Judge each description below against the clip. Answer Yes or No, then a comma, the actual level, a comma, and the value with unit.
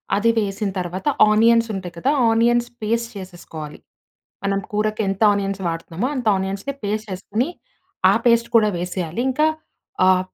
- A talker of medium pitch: No, high, 205 Hz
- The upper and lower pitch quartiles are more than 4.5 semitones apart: No, average, 3.7 semitones